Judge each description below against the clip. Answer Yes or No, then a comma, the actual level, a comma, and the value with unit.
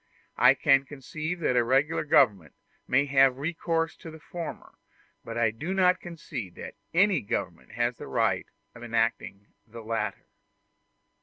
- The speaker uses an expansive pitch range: Yes, wide, 6.0 semitones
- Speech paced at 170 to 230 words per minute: No, average, 150 wpm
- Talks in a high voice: No, low, 135 Hz